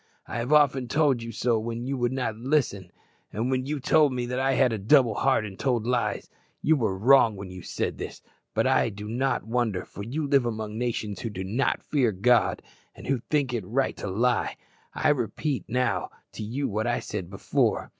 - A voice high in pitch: No, low, 120 Hz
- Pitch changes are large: No, average, 3.7 semitones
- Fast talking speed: Yes, fast, 210 wpm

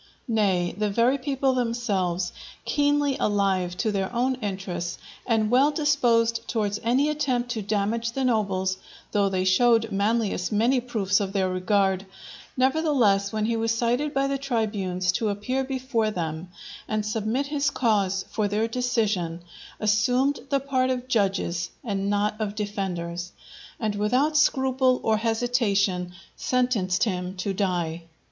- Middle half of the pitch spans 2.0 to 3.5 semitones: No, average, 4.4 semitones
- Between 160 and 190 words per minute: No, average, 140 wpm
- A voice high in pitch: Yes, high, 215 Hz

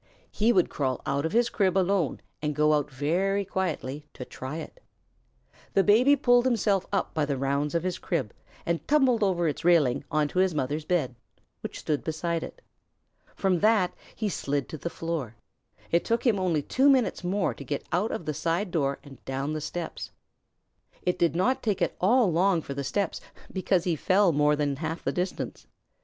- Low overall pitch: No, medium, 170 Hz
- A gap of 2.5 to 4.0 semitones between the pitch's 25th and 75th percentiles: No, average, 5.0 semitones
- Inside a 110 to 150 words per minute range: No, average, 190 wpm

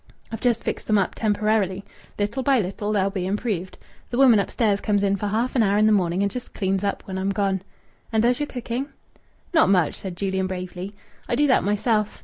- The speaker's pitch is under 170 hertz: No, high, 205 Hz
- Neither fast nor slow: No, fast, 215 wpm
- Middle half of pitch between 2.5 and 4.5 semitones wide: Yes, average, 3.1 semitones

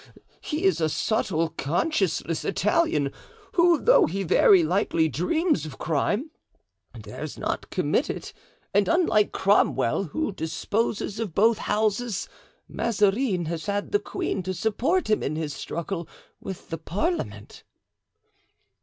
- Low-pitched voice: No, high, 195 Hz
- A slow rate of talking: Yes, slow, 130 wpm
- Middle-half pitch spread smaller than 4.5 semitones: No, wide, 5.5 semitones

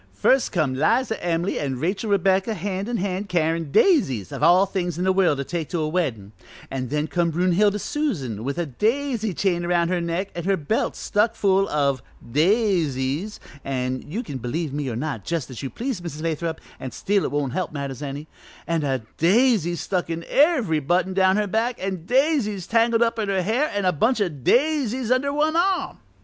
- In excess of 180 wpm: Yes, average, 200 wpm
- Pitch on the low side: No, medium, 180 Hz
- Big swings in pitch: Yes, wide, 6.1 semitones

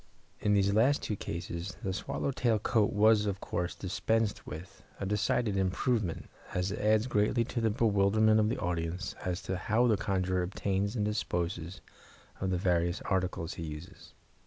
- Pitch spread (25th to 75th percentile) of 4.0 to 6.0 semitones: No, average, 3.1 semitones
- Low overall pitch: Yes, low, 100 Hz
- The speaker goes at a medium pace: Yes, average, 170 wpm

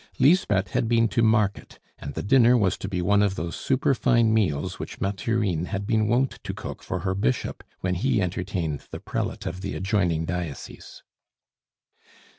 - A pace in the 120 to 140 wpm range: No, average, 170 wpm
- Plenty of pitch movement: No, average, 4.2 semitones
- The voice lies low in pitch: Yes, low, 100 Hz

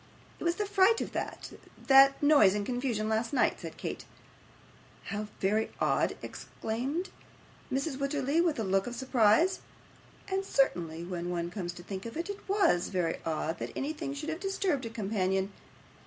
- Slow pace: No, average, 170 wpm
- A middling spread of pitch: No, wide, 8.3 semitones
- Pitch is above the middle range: Yes, high, 245 Hz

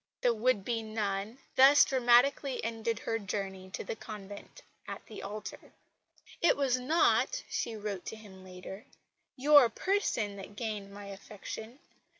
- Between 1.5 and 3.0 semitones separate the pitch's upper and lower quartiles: No, average, 3.9 semitones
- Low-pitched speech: No, high, 220 Hz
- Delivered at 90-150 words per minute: Yes, average, 145 wpm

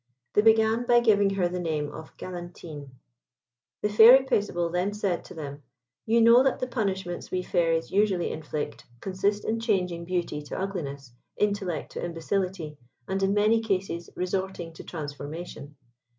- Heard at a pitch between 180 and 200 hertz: Yes, medium, 185 Hz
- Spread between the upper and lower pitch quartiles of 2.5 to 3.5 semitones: No, average, 3.9 semitones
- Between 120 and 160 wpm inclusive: Yes, average, 150 wpm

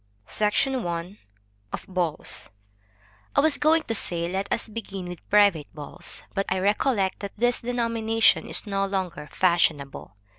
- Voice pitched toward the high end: Yes, high, 195 Hz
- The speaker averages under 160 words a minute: Yes, average, 145 wpm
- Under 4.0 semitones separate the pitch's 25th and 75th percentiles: No, average, 4.5 semitones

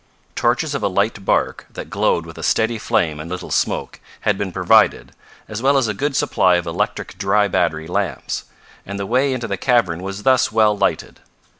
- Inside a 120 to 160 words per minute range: No, average, 195 wpm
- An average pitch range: Yes, average, 4.7 semitones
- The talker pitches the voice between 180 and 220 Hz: No, low, 100 Hz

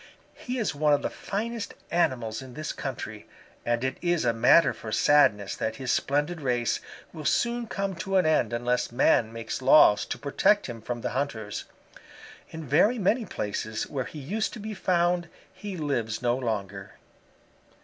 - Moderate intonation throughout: No, wide, 7.4 semitones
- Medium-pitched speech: Yes, medium, 145 Hz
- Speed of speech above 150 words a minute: Yes, average, 170 wpm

